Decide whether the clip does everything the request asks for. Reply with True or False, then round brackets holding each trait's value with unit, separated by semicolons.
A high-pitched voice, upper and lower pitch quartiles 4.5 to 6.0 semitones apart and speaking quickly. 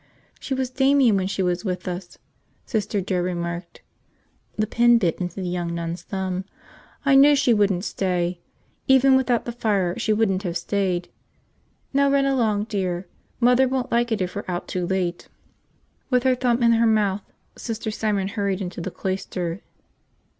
False (200 Hz; 4.8 semitones; 170 wpm)